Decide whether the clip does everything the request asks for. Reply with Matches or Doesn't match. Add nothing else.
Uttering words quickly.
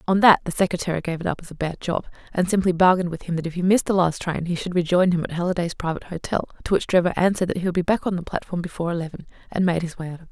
Matches